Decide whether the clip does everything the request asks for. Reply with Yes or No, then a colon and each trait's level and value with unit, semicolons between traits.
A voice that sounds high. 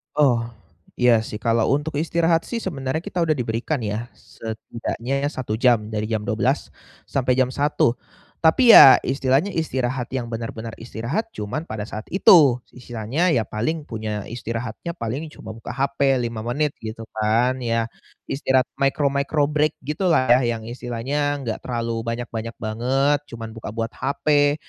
No: low, 125 Hz